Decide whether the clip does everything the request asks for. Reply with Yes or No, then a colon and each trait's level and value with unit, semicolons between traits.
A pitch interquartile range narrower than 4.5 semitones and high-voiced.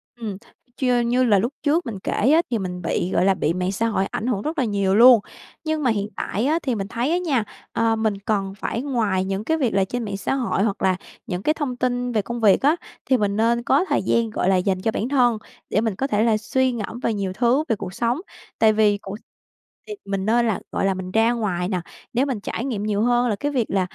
Yes: average, 3.9 semitones; high, 225 Hz